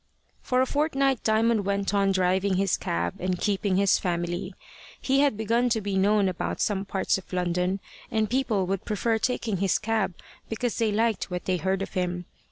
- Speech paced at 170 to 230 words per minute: Yes, average, 185 wpm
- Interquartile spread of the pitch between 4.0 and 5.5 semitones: No, average, 3.2 semitones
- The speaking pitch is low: No, high, 200 Hz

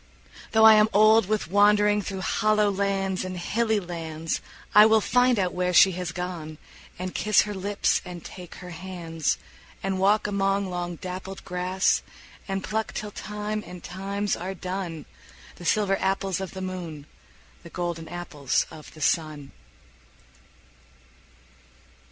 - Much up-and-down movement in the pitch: No, average, 2.8 semitones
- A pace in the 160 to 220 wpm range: No, average, 145 wpm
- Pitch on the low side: No, high, 190 Hz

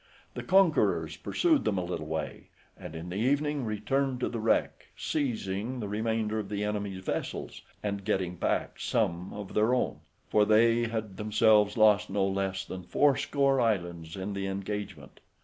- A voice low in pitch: Yes, low, 105 Hz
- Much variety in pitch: No, average, 3.3 semitones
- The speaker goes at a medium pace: Yes, average, 165 wpm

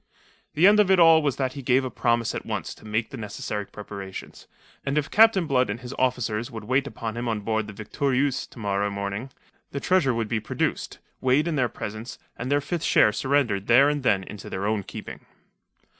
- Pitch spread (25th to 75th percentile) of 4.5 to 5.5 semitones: Yes, average, 4.8 semitones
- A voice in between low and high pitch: No, low, 125 Hz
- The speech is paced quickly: Yes, fast, 215 wpm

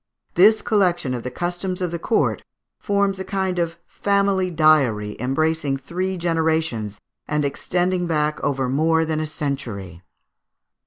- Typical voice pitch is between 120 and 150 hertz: No, medium, 160 Hz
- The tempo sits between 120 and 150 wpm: Yes, average, 140 wpm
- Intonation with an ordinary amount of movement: Yes, average, 4.7 semitones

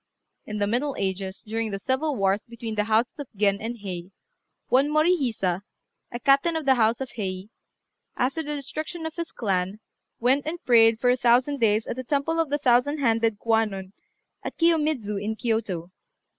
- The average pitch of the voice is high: Yes, high, 235 Hz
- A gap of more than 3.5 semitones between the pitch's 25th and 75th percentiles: Yes, average, 5.2 semitones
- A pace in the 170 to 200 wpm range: Yes, average, 180 wpm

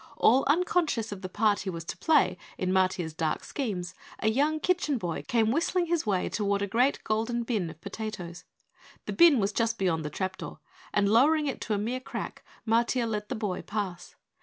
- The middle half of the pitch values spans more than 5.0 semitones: Yes, wide, 5.4 semitones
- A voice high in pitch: Yes, high, 220 Hz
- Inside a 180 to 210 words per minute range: Yes, average, 195 wpm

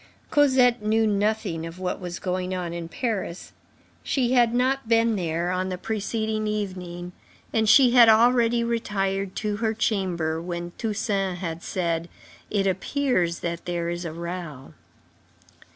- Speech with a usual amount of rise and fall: Yes, average, 4.5 semitones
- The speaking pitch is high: Yes, high, 195 Hz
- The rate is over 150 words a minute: No, average, 145 wpm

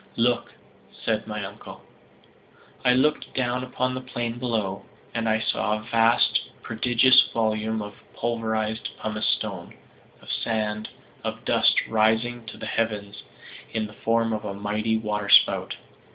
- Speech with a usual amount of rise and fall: No, narrow, 1.7 semitones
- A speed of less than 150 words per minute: Yes, average, 140 wpm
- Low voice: Yes, low, 110 Hz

